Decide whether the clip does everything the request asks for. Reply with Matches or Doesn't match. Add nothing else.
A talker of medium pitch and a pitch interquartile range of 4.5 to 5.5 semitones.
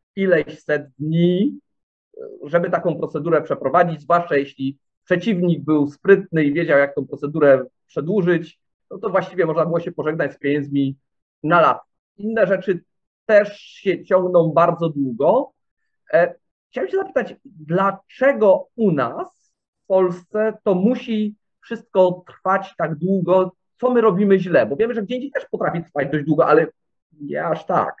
Matches